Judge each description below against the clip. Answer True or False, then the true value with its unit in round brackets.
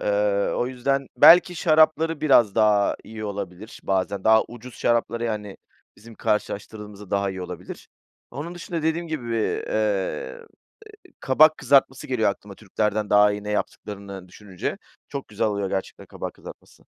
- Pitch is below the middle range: True (110 Hz)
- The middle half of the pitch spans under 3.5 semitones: False (4.7 semitones)